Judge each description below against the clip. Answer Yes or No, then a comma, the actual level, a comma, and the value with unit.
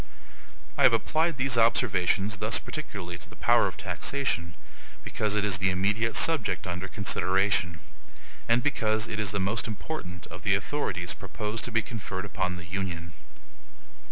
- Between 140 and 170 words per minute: Yes, average, 155 wpm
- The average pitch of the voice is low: Yes, low, 105 Hz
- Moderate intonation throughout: Yes, average, 3.6 semitones